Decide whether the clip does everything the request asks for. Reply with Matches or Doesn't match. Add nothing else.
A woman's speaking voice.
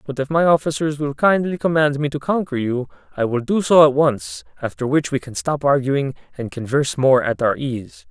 Doesn't match